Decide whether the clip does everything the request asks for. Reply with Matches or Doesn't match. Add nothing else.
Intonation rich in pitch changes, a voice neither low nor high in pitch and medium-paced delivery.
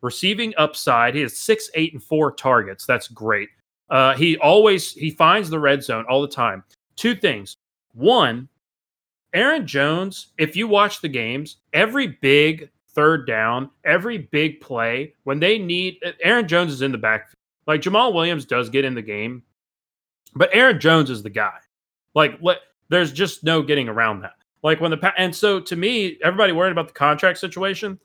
Matches